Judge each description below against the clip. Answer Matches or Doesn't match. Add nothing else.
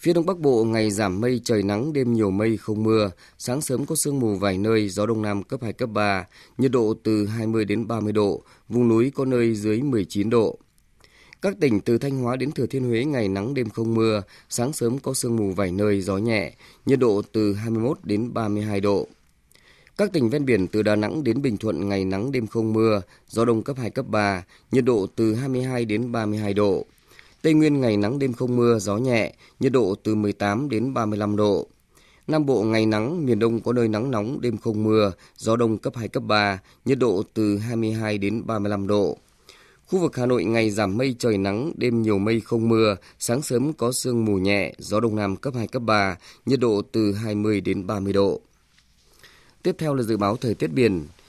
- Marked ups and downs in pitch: Doesn't match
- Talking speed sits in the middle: Matches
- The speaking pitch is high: Doesn't match